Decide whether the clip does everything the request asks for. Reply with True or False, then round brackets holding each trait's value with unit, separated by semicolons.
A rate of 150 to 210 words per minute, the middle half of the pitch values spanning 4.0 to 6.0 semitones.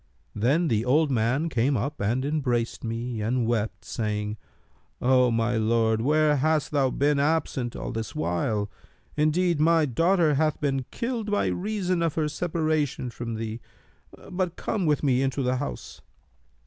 True (155 wpm; 5.1 semitones)